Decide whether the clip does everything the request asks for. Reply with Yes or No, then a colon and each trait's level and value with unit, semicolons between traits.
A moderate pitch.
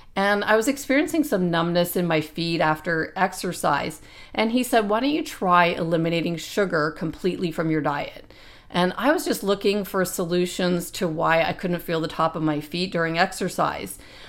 Yes: medium, 180 Hz